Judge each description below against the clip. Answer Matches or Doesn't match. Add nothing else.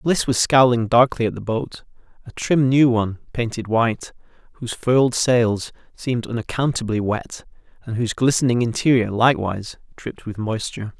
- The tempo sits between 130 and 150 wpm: Matches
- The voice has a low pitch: Matches